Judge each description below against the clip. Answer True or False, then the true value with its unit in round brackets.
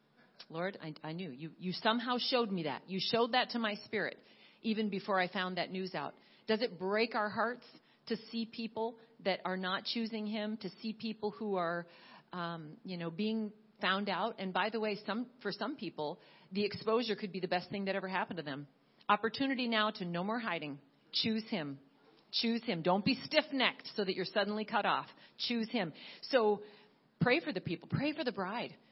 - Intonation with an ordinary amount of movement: True (3.5 semitones)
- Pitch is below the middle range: False (210 Hz)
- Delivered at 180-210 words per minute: True (200 wpm)